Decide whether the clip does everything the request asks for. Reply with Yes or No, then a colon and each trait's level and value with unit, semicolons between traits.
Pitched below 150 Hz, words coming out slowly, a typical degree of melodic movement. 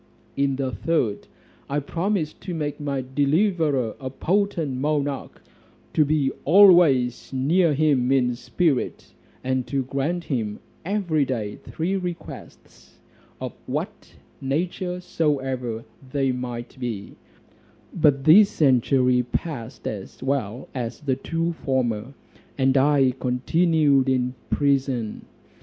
Yes: low, 135 Hz; slow, 115 wpm; average, 3.8 semitones